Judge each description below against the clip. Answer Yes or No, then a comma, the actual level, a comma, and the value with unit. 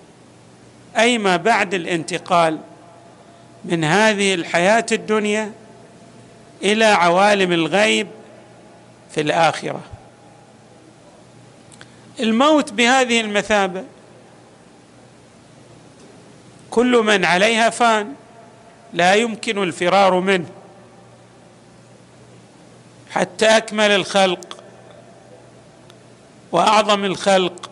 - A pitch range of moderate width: Yes, average, 3.9 semitones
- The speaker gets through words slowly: Yes, slow, 60 wpm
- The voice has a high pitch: Yes, high, 200 Hz